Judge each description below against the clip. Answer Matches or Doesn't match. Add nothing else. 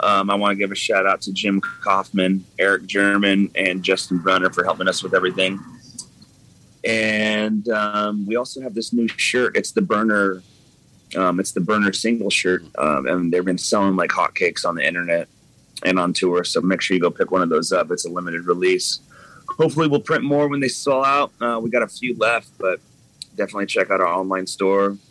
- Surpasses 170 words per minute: Matches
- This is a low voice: Matches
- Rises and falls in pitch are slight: Doesn't match